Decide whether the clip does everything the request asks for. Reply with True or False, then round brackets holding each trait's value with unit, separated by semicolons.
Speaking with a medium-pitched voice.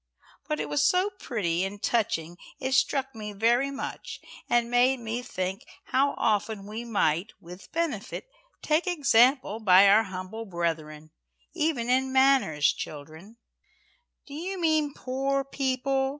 False (235 Hz)